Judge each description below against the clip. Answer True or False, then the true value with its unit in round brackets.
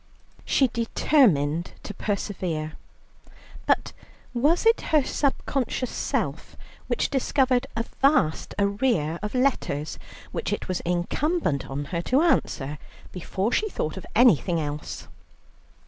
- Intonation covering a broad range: True (8.9 semitones)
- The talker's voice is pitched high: True (205 Hz)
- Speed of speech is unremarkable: False (115 wpm)